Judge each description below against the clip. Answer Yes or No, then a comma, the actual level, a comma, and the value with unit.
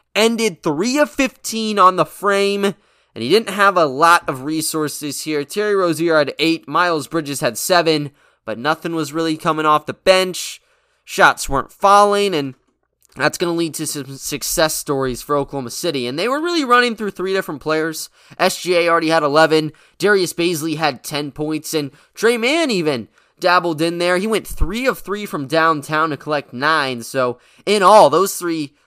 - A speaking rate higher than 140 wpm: Yes, average, 180 wpm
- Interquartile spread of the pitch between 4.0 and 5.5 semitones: Yes, average, 4.4 semitones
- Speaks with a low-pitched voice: No, medium, 165 Hz